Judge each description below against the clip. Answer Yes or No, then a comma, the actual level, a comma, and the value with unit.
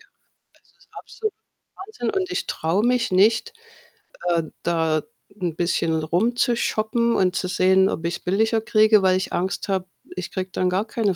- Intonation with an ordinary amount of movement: Yes, average, 4.4 semitones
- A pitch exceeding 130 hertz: Yes, high, 190 Hz